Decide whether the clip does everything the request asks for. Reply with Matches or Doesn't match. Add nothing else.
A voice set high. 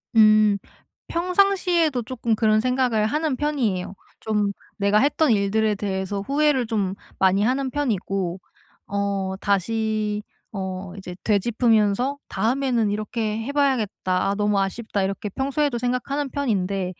Matches